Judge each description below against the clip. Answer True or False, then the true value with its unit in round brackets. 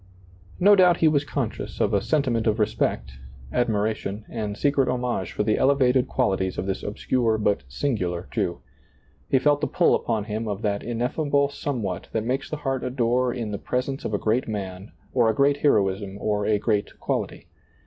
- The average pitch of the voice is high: False (115 Hz)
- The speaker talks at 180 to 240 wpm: True (190 wpm)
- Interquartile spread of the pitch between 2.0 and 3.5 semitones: False (4.6 semitones)